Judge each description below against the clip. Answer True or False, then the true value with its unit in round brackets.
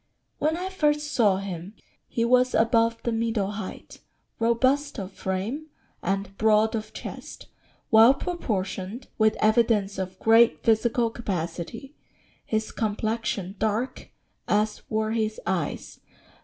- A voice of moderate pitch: False (220 Hz)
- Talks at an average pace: False (125 wpm)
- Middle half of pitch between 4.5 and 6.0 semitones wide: False (2.8 semitones)